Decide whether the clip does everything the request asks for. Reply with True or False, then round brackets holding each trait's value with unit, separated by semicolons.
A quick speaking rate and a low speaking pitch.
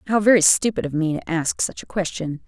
False (240 wpm; 180 Hz)